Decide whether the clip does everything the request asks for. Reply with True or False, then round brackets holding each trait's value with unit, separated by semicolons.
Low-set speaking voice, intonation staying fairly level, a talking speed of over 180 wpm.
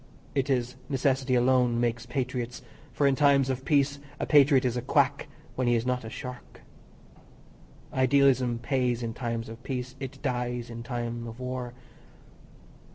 False (125 Hz; 1.8 semitones; 160 wpm)